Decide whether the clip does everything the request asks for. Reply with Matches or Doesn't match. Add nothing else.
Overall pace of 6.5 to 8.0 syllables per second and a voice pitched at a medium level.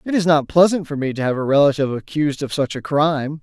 Matches